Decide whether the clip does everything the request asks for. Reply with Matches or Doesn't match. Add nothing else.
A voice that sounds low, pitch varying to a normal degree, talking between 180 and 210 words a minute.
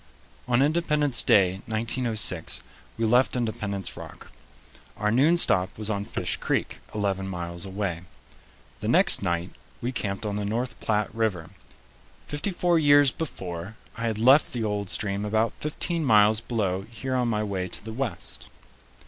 Doesn't match